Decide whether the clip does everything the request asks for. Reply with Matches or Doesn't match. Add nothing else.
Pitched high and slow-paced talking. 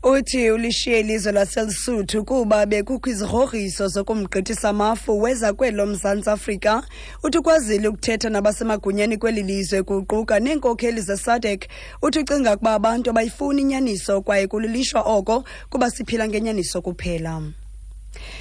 Matches